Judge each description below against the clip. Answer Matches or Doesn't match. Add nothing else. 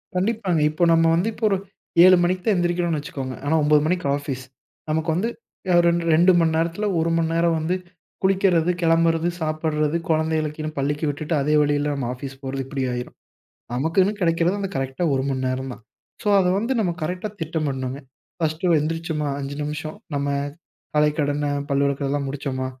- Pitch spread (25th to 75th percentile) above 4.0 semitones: Doesn't match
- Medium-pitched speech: Matches